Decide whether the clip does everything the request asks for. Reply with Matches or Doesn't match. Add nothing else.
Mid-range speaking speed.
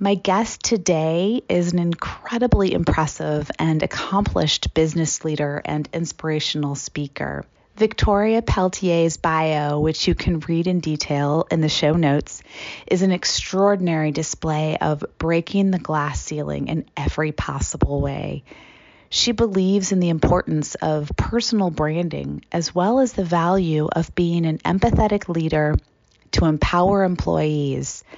Doesn't match